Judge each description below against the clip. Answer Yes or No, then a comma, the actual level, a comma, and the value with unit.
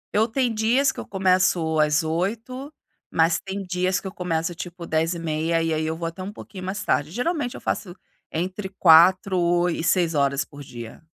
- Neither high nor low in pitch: Yes, medium, 175 Hz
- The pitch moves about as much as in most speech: Yes, average, 3.2 semitones